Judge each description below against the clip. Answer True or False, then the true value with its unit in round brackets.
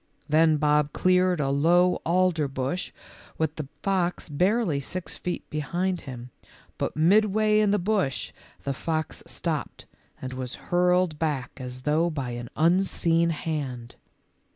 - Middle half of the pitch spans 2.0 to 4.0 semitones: False (4.5 semitones)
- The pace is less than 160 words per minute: True (135 wpm)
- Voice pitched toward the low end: False (160 Hz)